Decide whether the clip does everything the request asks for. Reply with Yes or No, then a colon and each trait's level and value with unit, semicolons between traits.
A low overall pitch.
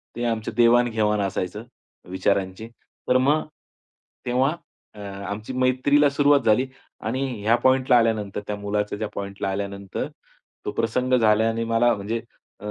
Yes: low, 110 Hz